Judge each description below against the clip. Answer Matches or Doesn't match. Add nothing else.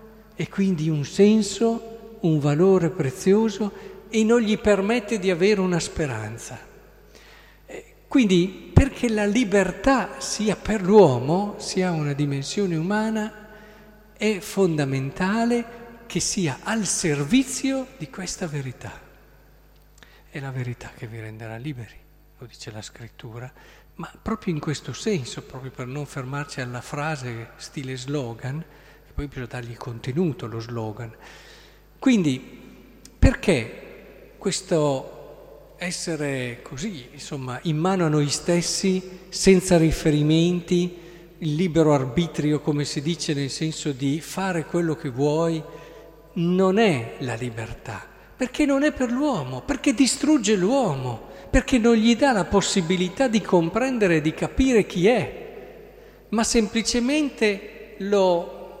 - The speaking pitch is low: Doesn't match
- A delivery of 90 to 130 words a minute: Matches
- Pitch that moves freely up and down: Matches